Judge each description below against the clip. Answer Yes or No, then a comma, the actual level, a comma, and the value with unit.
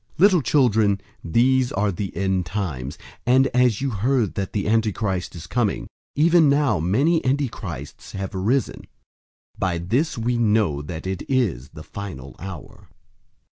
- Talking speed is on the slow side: No, average, 145 wpm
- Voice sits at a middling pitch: No, low, 105 Hz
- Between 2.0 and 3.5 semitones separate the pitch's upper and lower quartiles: No, wide, 5.6 semitones